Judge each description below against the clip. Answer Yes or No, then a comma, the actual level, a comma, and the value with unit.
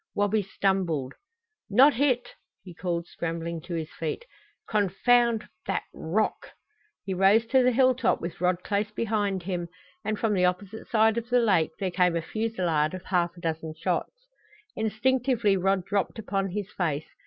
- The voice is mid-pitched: No, high, 195 Hz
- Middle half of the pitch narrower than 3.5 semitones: No, average, 4.3 semitones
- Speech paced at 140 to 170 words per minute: Yes, average, 160 wpm